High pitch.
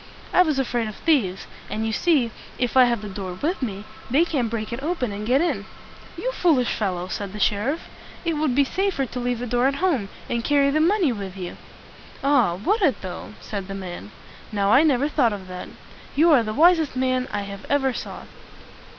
Yes: high, 245 Hz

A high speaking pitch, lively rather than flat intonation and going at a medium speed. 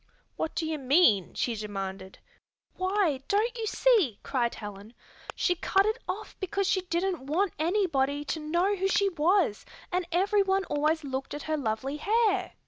Yes: very high, 335 Hz; wide, 6.5 semitones; average, 160 wpm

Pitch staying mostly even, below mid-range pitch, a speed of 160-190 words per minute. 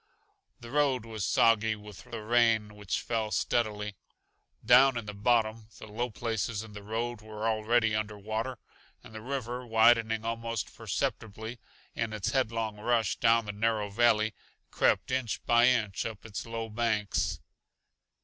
No: narrow, 1.7 semitones; low, 110 Hz; average, 150 wpm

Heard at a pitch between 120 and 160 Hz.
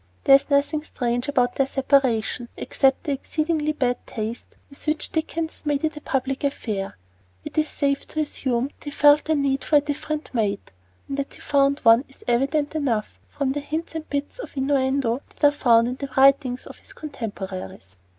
No: very high, 275 Hz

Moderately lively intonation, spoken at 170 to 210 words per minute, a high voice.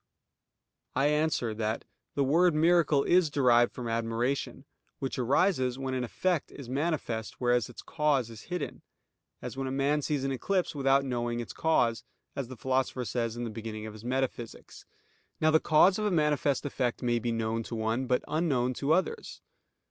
No: average, 4.1 semitones; average, 180 wpm; low, 130 Hz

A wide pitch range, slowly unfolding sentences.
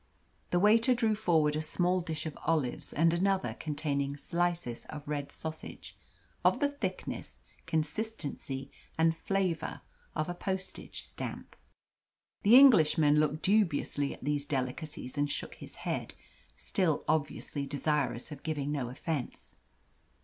No: average, 3.7 semitones; slow, 130 wpm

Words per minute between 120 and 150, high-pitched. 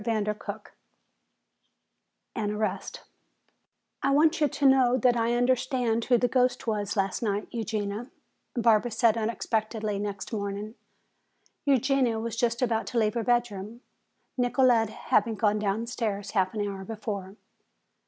Yes: slow, 135 wpm; high, 225 Hz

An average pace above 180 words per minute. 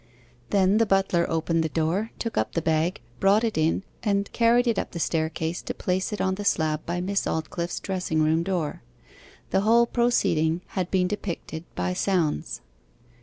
No: average, 175 wpm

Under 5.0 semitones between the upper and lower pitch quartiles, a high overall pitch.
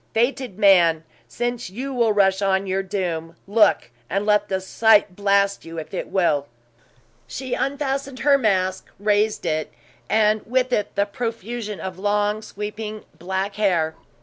Yes: average, 2.9 semitones; high, 205 Hz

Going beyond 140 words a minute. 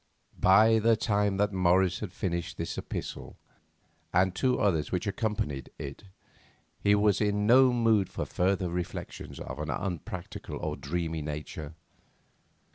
No: slow, 135 wpm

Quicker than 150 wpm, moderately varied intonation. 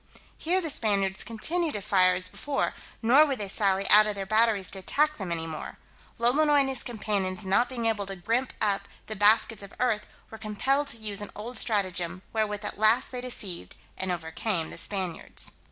Yes: average, 195 wpm; average, 4.0 semitones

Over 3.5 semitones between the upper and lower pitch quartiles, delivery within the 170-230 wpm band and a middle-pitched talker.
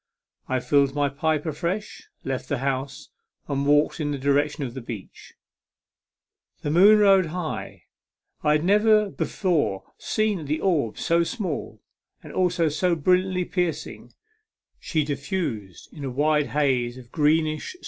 No: average, 4.4 semitones; average, 140 wpm; medium, 150 Hz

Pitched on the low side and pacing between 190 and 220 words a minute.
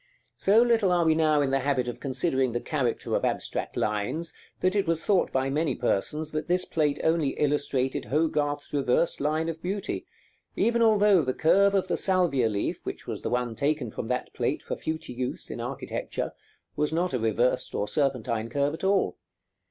No: medium, 150 Hz; average, 195 wpm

